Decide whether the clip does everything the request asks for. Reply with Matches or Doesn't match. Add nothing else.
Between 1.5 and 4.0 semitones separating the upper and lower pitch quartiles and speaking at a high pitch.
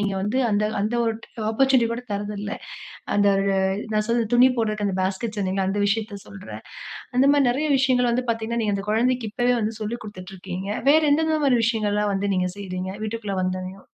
Matches